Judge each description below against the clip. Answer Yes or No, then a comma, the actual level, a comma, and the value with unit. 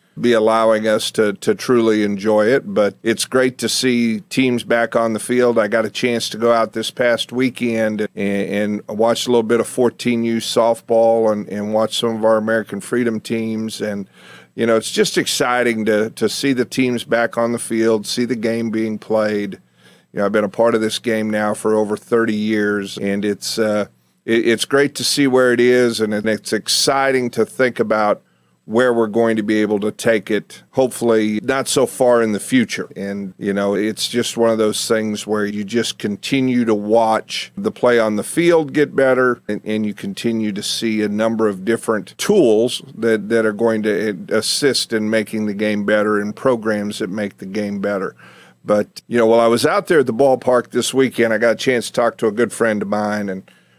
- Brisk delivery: Yes, fast, 215 wpm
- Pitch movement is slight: Yes, narrow, 2.1 semitones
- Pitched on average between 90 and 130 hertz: Yes, low, 110 Hz